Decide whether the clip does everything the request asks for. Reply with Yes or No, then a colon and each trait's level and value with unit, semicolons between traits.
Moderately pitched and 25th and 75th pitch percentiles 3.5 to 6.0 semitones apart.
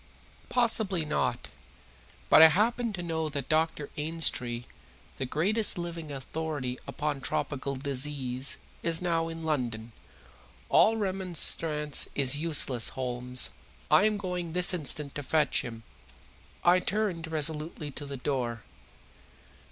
Yes: medium, 155 Hz; average, 4.1 semitones